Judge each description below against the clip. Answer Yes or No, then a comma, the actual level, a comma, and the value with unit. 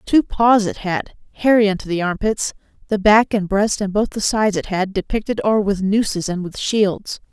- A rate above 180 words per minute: Yes, fast, 205 wpm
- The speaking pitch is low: No, high, 205 Hz